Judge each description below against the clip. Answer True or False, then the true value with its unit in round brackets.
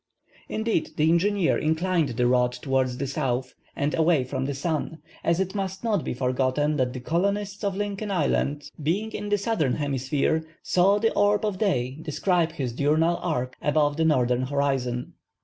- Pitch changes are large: True (6.3 semitones)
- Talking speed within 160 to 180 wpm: True (170 wpm)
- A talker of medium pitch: True (155 Hz)